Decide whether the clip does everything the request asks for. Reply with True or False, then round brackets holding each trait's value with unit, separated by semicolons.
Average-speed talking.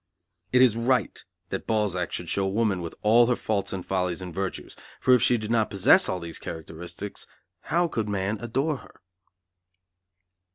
True (170 wpm)